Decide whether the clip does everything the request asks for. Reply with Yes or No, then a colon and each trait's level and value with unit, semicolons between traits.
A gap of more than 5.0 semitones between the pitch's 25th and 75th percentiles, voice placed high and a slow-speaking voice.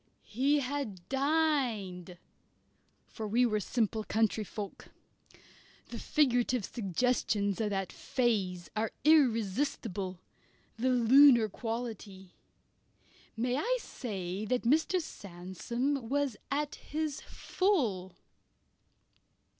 Yes: wide, 5.5 semitones; high, 230 Hz; slow, 90 wpm